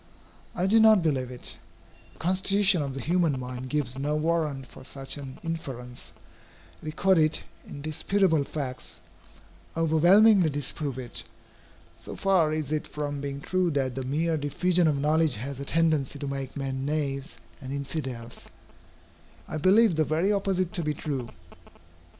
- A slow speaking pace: No, average, 145 wpm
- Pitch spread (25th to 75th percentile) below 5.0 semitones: Yes, average, 3.7 semitones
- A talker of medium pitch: Yes, medium, 150 Hz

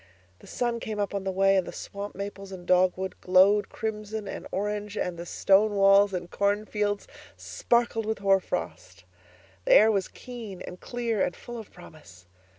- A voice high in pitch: Yes, high, 200 Hz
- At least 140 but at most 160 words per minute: No, average, 175 wpm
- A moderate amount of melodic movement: No, narrow, 2.2 semitones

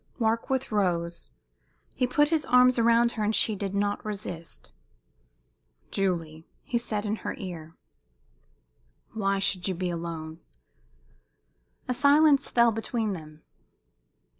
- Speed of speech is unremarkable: No, slow, 120 wpm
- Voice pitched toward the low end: No, high, 205 Hz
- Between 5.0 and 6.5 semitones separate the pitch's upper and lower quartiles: Yes, average, 5.3 semitones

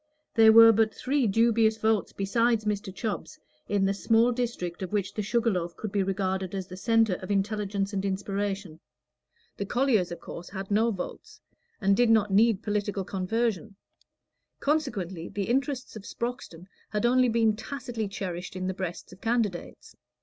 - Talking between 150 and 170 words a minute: Yes, average, 165 wpm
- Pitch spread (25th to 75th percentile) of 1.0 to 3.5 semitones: Yes, average, 3.0 semitones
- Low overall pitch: No, high, 205 Hz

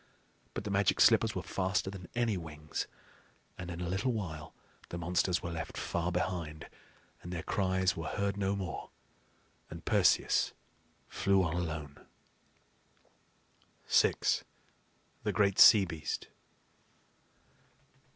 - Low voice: Yes, very low, 90 Hz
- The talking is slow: Yes, slow, 120 wpm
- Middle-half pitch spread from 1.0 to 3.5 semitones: Yes, average, 2.7 semitones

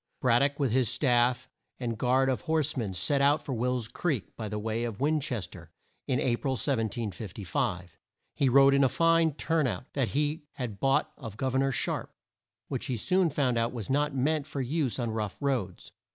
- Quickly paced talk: Yes, fast, 210 wpm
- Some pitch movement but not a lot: Yes, average, 3.6 semitones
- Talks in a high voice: No, low, 130 Hz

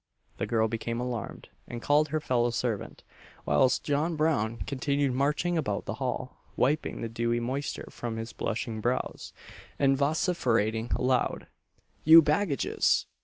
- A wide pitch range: No, average, 4.1 semitones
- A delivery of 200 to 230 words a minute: No, slow, 135 wpm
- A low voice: Yes, low, 125 Hz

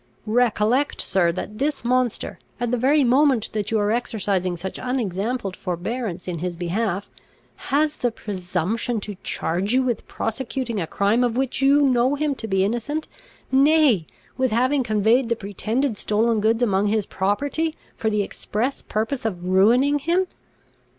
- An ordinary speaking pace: Yes, average, 155 wpm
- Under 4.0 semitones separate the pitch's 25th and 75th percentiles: No, average, 4.5 semitones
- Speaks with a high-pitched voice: Yes, high, 225 Hz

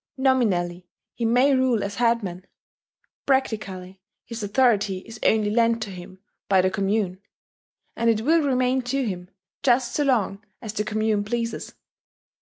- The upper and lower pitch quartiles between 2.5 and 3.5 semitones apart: No, average, 3.9 semitones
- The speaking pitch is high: Yes, high, 220 Hz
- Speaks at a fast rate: No, average, 145 wpm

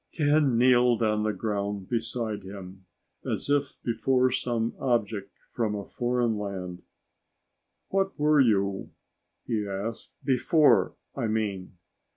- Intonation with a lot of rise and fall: No, average, 3.9 semitones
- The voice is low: Yes, low, 115 Hz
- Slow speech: Yes, slow, 125 wpm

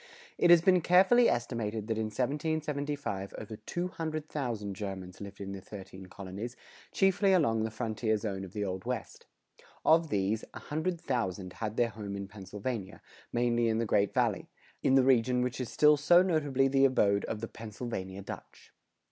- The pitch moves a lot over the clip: Yes, wide, 6.3 semitones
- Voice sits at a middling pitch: No, low, 115 Hz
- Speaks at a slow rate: No, average, 170 wpm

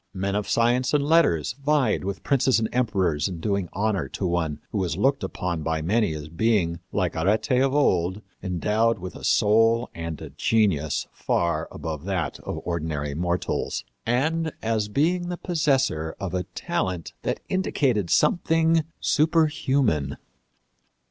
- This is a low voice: Yes, low, 105 Hz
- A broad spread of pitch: Yes, wide, 7.8 semitones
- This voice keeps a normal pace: Yes, average, 150 wpm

